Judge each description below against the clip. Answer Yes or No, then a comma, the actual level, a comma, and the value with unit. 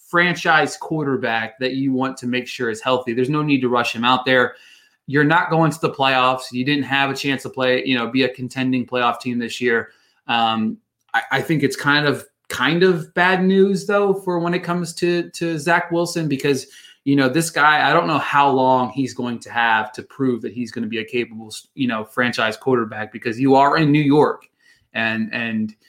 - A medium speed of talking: No, fast, 220 wpm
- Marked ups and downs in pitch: No, average, 4.4 semitones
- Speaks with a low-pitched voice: Yes, low, 130 Hz